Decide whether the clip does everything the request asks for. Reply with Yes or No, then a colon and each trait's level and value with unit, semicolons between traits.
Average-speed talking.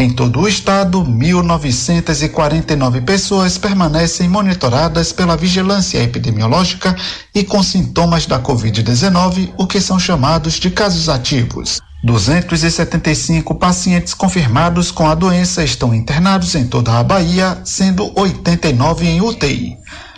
No: slow, 115 wpm